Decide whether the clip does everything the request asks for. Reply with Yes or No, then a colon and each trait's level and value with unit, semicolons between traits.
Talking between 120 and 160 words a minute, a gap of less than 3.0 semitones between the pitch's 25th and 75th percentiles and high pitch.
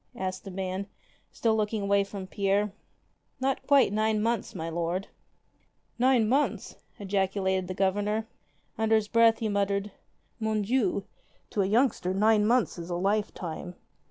Yes: average, 145 wpm; narrow, 2.5 semitones; high, 205 Hz